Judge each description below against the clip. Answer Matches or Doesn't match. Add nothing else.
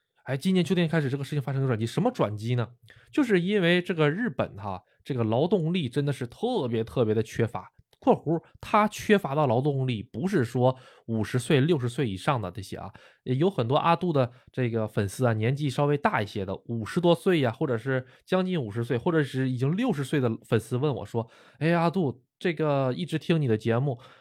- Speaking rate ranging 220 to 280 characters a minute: Doesn't match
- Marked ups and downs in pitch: Matches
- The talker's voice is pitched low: Matches